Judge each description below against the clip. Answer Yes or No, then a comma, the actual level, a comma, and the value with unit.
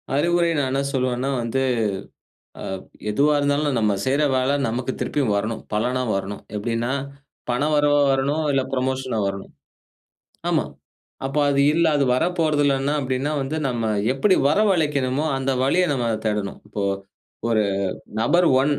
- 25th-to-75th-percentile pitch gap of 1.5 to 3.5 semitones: Yes, average, 3.2 semitones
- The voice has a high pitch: No, low, 135 Hz